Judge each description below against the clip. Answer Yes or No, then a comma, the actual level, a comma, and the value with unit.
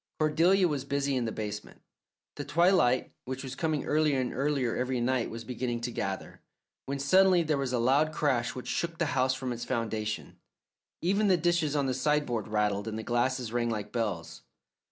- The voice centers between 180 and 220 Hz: No, low, 130 Hz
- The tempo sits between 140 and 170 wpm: No, average, 190 wpm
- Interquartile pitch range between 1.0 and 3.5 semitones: No, average, 4.3 semitones